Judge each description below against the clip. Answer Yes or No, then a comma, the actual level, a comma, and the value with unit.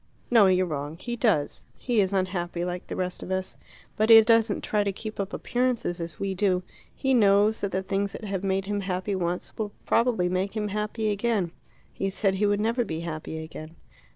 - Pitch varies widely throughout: No, average, 3.0 semitones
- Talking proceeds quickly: Yes, fast, 210 wpm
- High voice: Yes, high, 195 Hz